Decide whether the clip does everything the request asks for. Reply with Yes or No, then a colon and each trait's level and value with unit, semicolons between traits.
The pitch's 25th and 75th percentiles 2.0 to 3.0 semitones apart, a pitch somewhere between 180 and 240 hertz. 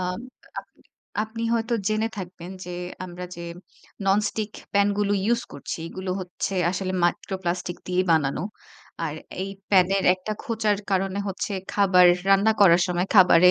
Yes: narrow, 2.4 semitones; high, 190 Hz